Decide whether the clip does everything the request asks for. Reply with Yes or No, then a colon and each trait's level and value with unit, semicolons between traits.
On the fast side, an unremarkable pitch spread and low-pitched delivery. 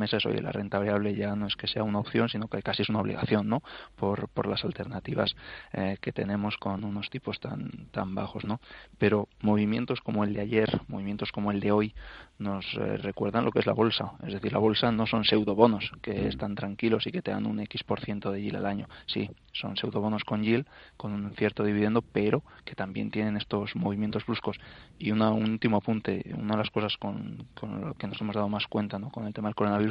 No: fast, 230 wpm; narrow, 1.2 semitones; low, 105 Hz